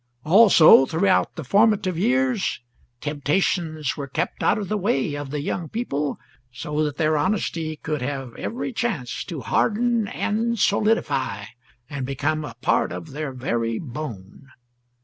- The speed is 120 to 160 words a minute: Yes, average, 145 wpm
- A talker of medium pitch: Yes, medium, 155 Hz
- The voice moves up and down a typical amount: No, wide, 6.5 semitones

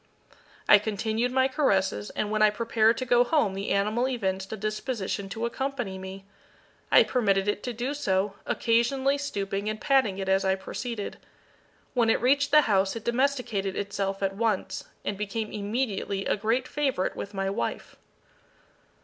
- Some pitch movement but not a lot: Yes, average, 4.0 semitones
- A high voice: Yes, high, 215 Hz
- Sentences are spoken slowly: No, average, 165 wpm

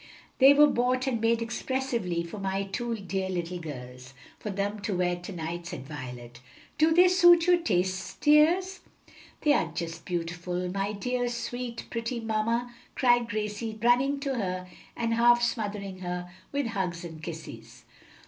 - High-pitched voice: Yes, high, 210 Hz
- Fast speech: No, average, 160 wpm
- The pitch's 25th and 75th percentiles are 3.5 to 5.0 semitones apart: No, wide, 5.5 semitones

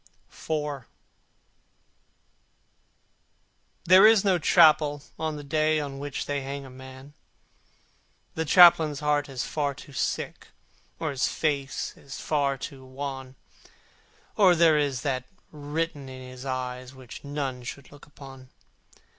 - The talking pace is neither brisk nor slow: No, slow, 130 wpm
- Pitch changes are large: No, narrow, 2.6 semitones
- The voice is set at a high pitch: No, medium, 140 Hz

